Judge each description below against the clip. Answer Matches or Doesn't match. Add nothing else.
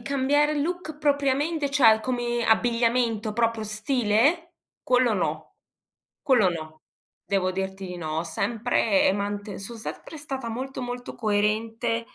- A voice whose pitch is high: Matches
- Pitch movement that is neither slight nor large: Matches